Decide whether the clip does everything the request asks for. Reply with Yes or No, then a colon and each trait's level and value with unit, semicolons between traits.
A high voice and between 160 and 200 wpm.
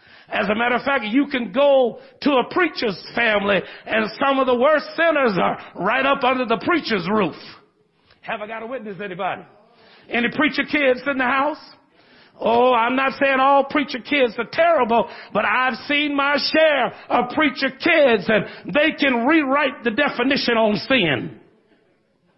Yes: very high, 255 Hz; average, 165 wpm